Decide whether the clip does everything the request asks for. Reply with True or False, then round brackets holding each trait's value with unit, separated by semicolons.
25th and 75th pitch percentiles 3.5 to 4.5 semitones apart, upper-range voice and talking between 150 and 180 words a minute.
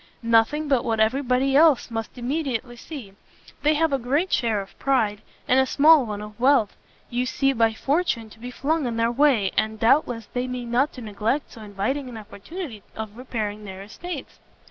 False (4.0 semitones; 245 Hz; 190 wpm)